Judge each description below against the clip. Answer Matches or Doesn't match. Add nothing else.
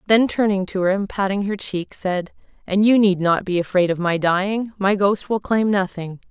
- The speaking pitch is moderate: Doesn't match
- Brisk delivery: Matches